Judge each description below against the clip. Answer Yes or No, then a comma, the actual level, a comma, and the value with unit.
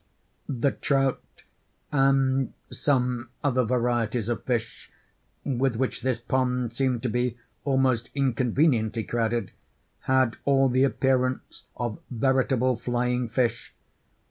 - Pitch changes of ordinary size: No, narrow, 1.8 semitones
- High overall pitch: No, low, 125 Hz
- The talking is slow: Yes, slow, 110 wpm